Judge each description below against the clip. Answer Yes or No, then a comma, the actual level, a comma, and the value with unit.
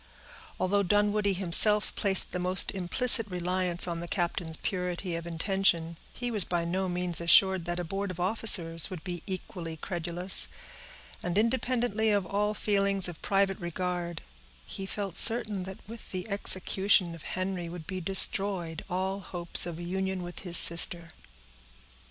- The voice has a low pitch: No, medium, 185 Hz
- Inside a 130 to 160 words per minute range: Yes, average, 155 wpm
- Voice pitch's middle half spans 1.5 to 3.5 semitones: Yes, narrow, 2.4 semitones